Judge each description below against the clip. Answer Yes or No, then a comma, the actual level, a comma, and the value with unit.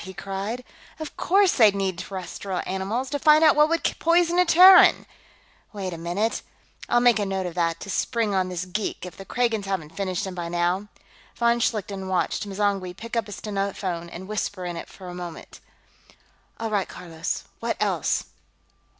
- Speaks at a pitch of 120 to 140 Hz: No, high, 195 Hz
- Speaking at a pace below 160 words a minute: No, average, 185 wpm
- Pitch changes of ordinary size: Yes, average, 4.2 semitones